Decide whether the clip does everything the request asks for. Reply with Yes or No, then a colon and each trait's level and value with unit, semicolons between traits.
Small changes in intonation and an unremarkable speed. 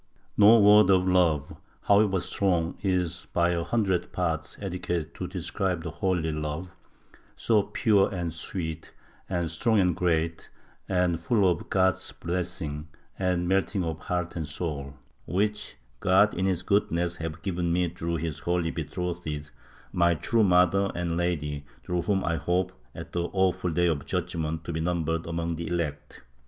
Yes: narrow, 2.2 semitones; average, 160 wpm